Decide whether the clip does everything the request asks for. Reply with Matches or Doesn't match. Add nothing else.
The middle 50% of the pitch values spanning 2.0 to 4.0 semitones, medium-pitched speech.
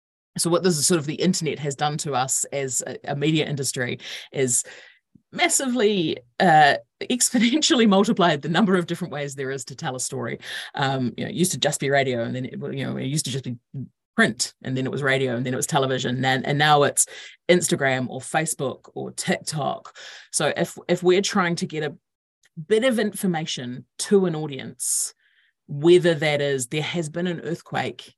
Doesn't match